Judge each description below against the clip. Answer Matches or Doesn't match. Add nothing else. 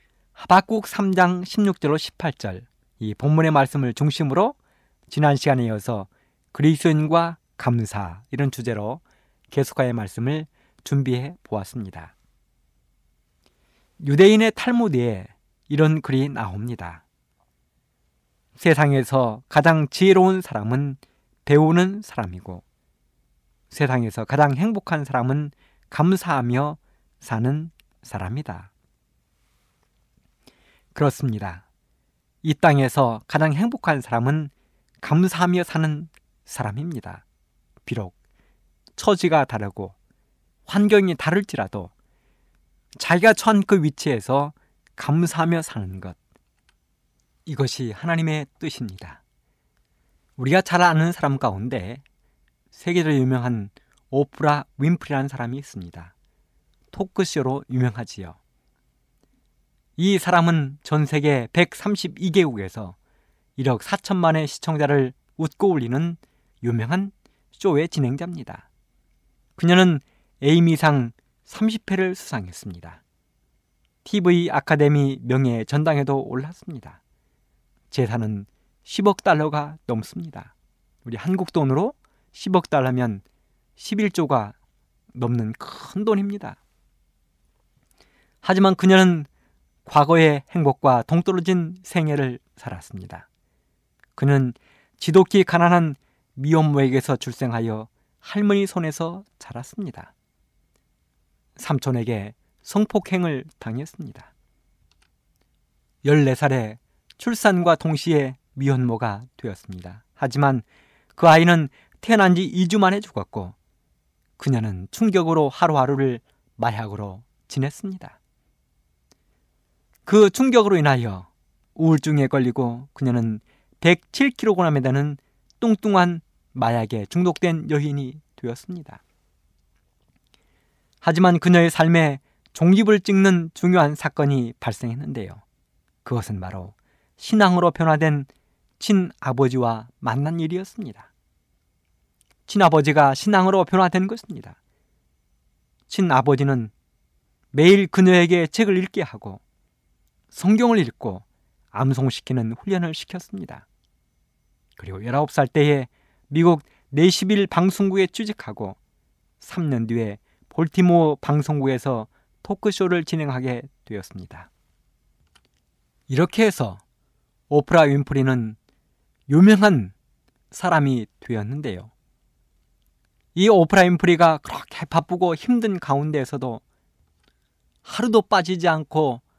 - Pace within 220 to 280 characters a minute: Matches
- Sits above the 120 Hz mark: Matches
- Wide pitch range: Matches